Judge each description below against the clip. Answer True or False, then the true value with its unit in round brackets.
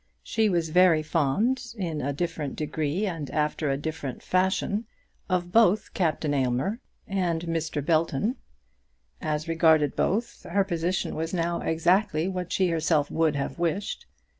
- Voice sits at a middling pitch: True (165 Hz)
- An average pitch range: True (3.3 semitones)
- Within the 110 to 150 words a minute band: True (140 wpm)